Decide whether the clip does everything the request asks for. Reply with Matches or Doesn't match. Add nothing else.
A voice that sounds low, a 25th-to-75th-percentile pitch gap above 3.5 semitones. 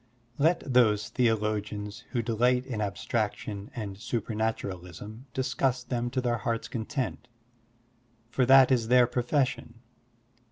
Doesn't match